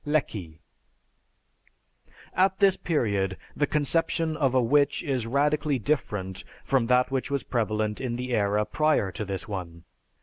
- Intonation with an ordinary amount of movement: No, wide, 6.1 semitones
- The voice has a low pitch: Yes, low, 125 Hz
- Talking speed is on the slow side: No, average, 145 wpm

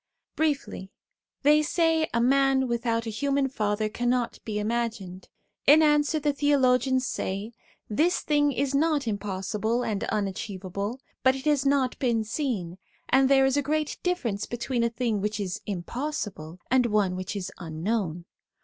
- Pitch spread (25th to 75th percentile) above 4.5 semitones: Yes, average, 5.1 semitones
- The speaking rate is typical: Yes, average, 160 wpm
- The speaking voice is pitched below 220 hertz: No, high, 240 Hz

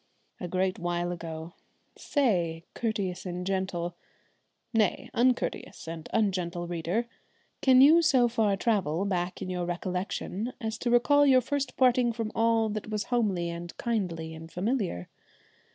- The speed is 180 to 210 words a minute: No, average, 140 wpm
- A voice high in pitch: Yes, high, 195 Hz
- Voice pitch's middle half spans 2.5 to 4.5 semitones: No, average, 5.3 semitones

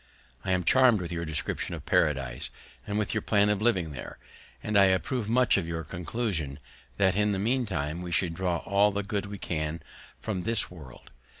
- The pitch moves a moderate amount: Yes, average, 4.1 semitones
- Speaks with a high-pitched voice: No, very low, 95 Hz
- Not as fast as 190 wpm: No, average, 195 wpm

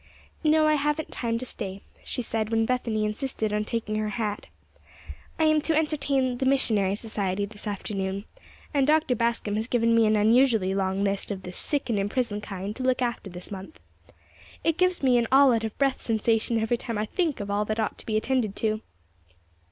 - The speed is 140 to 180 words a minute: No, fast, 205 wpm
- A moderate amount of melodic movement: Yes, average, 4.0 semitones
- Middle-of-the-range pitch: No, high, 225 Hz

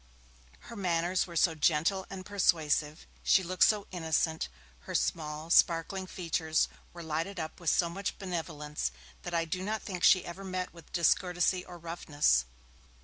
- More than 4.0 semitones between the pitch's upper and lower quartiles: No, narrow, 2.5 semitones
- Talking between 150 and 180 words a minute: Yes, average, 155 wpm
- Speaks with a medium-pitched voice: Yes, medium, 170 Hz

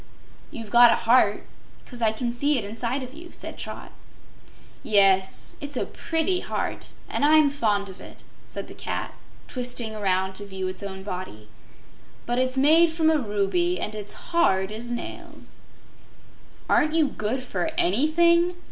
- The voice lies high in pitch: Yes, high, 240 Hz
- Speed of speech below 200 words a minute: Yes, average, 160 wpm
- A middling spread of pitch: No, wide, 7.0 semitones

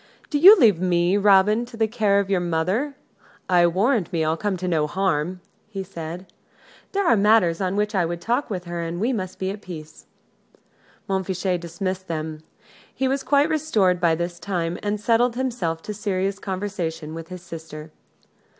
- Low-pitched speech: No, medium, 185 Hz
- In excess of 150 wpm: Yes, average, 185 wpm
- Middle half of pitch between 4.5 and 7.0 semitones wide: No, average, 3.6 semitones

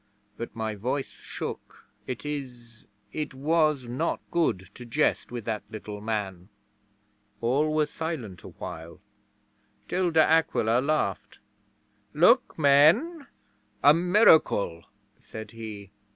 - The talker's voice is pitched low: Yes, low, 130 Hz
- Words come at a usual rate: No, slow, 110 wpm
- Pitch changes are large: Yes, wide, 6.3 semitones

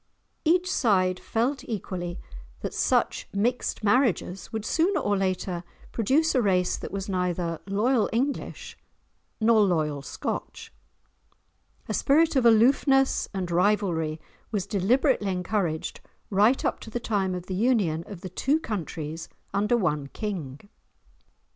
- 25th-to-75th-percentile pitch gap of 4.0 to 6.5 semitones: Yes, average, 4.9 semitones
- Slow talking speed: Yes, slow, 130 wpm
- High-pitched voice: Yes, high, 200 Hz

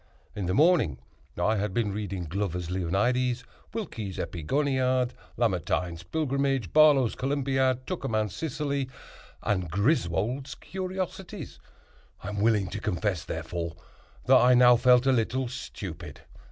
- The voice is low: Yes, low, 120 Hz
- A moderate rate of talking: No, slow, 120 wpm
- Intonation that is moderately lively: No, wide, 6.2 semitones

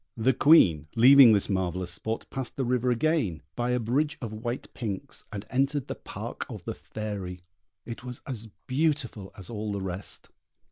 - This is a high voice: No, low, 115 Hz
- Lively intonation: No, average, 4.6 semitones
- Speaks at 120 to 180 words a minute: Yes, average, 175 wpm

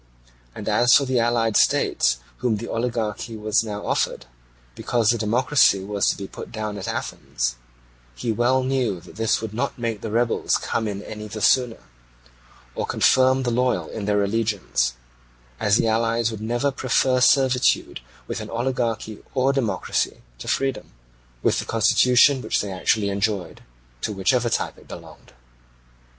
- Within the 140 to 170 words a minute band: Yes, average, 160 wpm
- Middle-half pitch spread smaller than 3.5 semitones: Yes, average, 3.1 semitones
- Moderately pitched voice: No, low, 115 Hz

